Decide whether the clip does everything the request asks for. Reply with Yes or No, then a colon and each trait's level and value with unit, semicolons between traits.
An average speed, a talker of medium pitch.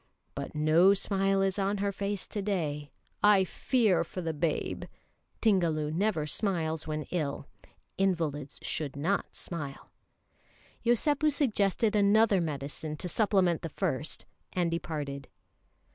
No: slow, 125 wpm; medium, 180 Hz